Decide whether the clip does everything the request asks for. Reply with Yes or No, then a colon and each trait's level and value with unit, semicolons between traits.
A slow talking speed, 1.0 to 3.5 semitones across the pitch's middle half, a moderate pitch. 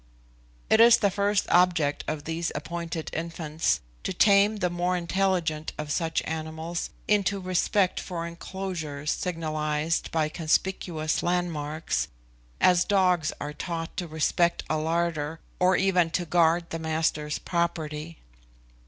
Yes: slow, 125 wpm; narrow, 2.4 semitones; medium, 170 Hz